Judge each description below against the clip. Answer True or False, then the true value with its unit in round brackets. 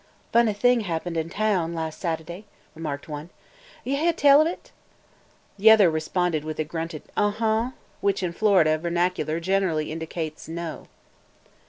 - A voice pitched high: False (170 Hz)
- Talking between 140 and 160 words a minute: True (150 wpm)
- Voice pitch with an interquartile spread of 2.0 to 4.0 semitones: False (4.7 semitones)